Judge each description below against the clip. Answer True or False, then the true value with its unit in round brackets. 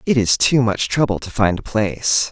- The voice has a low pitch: True (115 Hz)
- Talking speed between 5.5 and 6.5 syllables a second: False (5.0 syllables/s)